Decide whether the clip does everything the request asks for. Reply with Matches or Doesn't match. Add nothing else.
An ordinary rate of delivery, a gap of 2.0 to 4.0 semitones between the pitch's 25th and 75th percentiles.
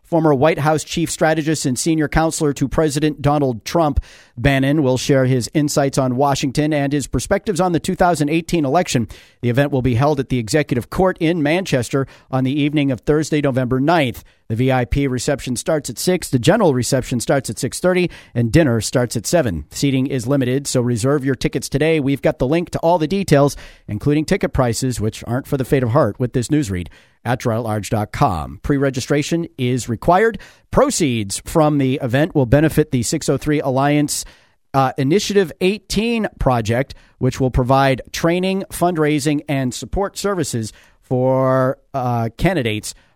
Matches